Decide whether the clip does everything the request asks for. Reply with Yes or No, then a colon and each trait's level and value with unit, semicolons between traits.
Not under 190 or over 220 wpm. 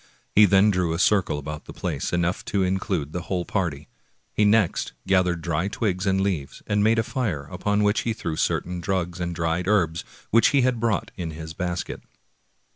Yes: average, 195 wpm